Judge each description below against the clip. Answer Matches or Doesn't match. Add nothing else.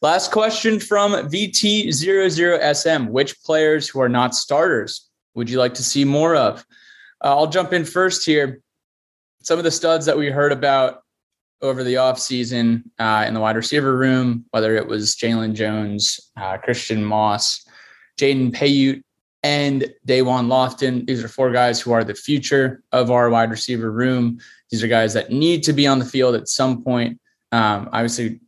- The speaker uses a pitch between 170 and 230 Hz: Doesn't match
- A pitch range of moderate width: Matches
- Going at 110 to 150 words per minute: Doesn't match